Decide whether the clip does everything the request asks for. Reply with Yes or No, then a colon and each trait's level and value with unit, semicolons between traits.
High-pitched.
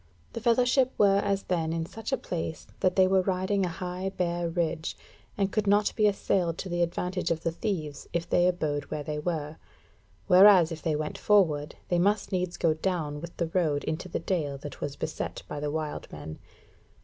No: medium, 175 Hz